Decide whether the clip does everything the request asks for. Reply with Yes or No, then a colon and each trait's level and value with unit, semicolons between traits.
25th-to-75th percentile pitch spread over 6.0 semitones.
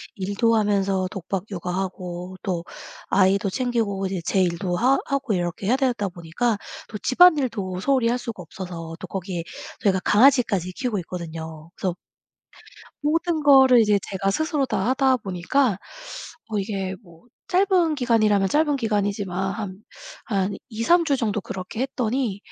No: average, 5.3 semitones